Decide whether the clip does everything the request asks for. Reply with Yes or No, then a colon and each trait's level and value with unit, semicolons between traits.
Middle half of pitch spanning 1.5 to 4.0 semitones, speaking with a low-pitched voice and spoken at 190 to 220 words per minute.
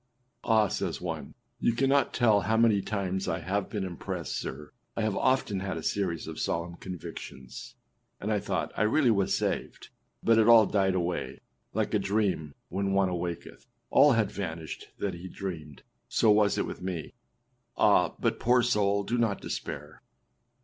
No: average, 3.6 semitones; low, 100 Hz; average, 175 wpm